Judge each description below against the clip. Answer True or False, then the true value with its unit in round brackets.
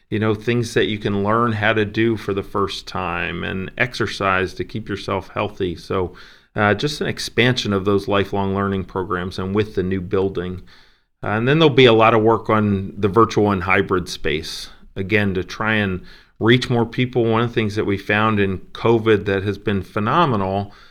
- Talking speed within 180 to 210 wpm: True (200 wpm)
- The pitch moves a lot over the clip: False (2.6 semitones)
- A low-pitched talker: True (105 Hz)